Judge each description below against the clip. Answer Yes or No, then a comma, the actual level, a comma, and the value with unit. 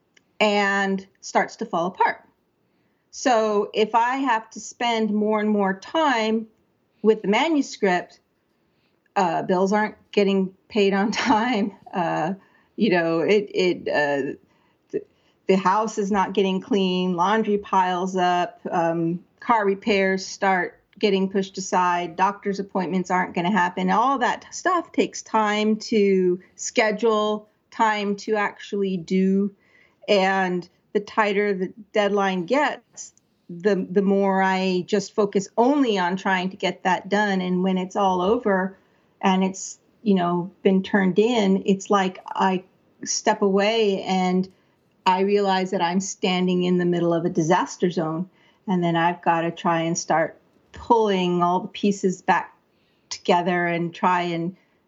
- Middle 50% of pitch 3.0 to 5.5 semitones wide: No, narrow, 2.6 semitones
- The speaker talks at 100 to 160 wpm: Yes, average, 140 wpm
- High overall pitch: Yes, high, 195 Hz